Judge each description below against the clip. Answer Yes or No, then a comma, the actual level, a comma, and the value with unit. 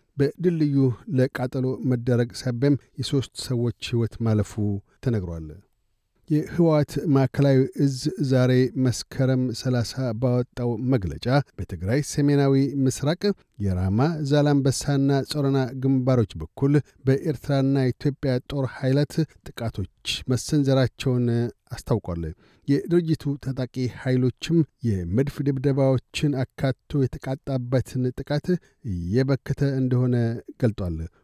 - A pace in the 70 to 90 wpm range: Yes, average, 85 wpm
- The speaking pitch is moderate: No, low, 130 Hz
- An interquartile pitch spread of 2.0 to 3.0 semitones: Yes, average, 2.7 semitones